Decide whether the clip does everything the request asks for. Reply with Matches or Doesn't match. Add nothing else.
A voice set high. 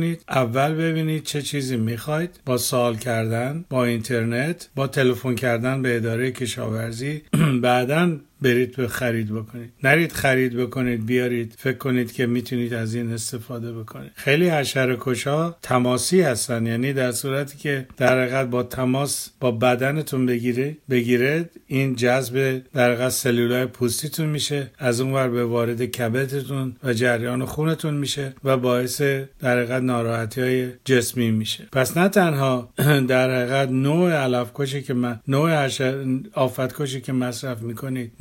Doesn't match